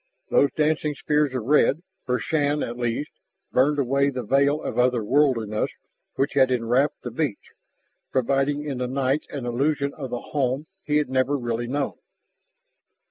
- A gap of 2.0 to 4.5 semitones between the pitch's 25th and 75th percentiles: Yes, average, 2.8 semitones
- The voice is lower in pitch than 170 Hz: Yes, low, 135 Hz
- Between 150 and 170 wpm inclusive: Yes, average, 160 wpm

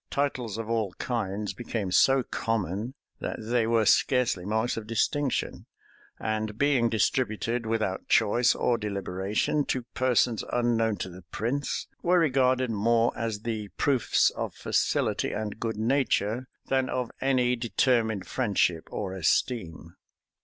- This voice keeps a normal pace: No, slow, 130 wpm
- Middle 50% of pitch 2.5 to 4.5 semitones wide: Yes, average, 3.1 semitones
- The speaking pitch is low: Yes, low, 115 Hz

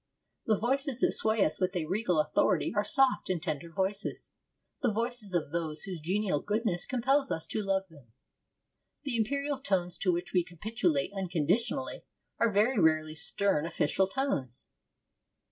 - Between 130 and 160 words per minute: Yes, average, 155 wpm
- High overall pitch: Yes, high, 195 Hz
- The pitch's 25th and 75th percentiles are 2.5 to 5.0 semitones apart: No, wide, 5.5 semitones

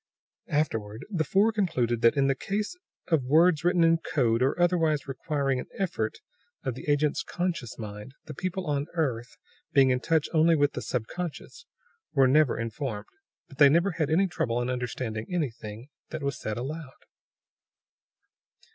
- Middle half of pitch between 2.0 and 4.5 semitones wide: No, average, 5.1 semitones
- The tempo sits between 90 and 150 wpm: No, average, 165 wpm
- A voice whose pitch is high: No, medium, 145 Hz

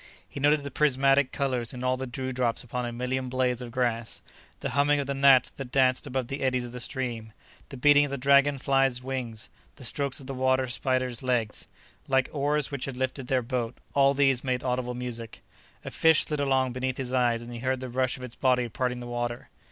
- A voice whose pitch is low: Yes, low, 130 Hz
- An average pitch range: No, narrow, 1.7 semitones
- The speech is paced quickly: Yes, fast, 215 wpm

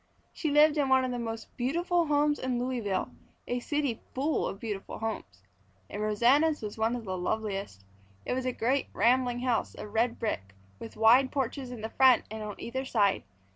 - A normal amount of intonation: Yes, average, 3.4 semitones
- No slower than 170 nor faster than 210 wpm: Yes, average, 190 wpm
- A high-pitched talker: Yes, high, 245 Hz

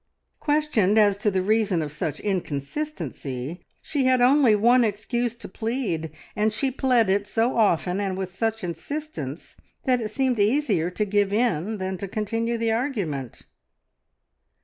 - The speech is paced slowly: No, average, 150 wpm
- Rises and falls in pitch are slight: No, average, 4.5 semitones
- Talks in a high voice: Yes, high, 215 Hz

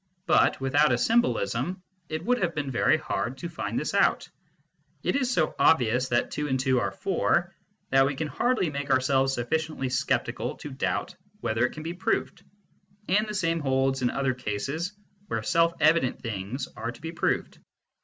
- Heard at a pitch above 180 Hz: No, medium, 140 Hz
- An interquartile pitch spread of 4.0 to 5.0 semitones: Yes, average, 4.5 semitones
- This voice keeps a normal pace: Yes, average, 180 wpm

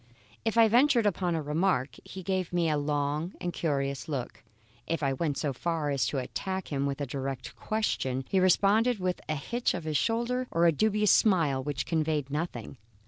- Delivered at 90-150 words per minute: No, average, 195 wpm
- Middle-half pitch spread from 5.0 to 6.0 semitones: Yes, average, 5.3 semitones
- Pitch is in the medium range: Yes, medium, 165 Hz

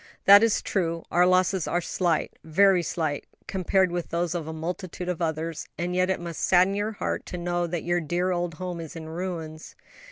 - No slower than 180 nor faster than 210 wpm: Yes, average, 195 wpm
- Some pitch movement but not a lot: No, narrow, 1.8 semitones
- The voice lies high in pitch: No, medium, 175 Hz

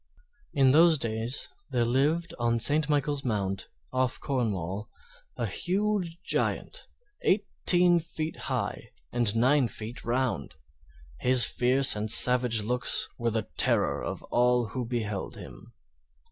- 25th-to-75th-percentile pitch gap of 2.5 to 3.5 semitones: No, average, 4.4 semitones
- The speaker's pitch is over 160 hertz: No, low, 125 Hz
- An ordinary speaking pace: No, slow, 125 wpm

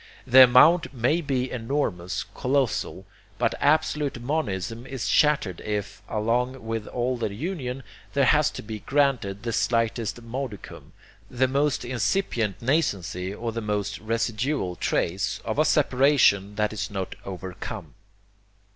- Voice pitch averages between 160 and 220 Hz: No, low, 120 Hz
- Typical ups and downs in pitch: Yes, average, 4.6 semitones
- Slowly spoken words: Yes, slow, 130 wpm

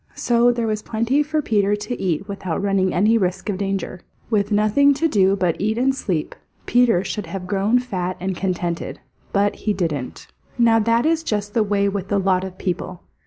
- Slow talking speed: No, average, 195 wpm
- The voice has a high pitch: Yes, high, 205 Hz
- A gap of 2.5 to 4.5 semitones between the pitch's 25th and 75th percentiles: Yes, average, 3.5 semitones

